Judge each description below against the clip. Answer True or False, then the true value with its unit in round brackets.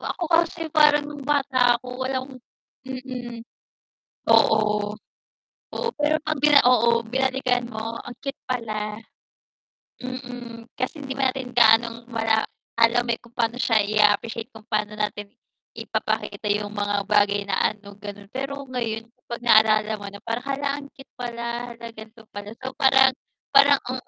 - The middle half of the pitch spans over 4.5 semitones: False (3.4 semitones)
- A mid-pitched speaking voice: False (235 Hz)